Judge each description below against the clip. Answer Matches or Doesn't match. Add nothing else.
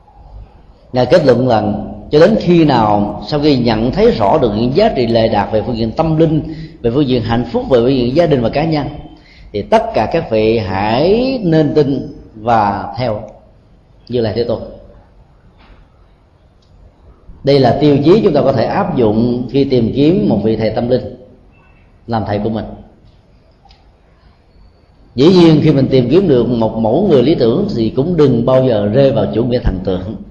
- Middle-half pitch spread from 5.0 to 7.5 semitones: Matches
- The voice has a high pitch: Doesn't match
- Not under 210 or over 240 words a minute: Doesn't match